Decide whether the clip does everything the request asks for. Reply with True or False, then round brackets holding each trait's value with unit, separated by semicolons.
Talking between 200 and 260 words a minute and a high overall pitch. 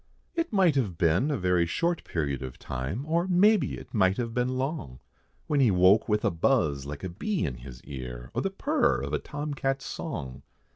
False (205 wpm; 100 Hz)